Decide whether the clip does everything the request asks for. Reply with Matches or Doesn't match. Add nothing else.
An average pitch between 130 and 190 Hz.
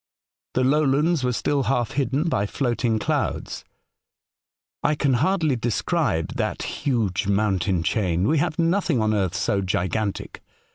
Doesn't match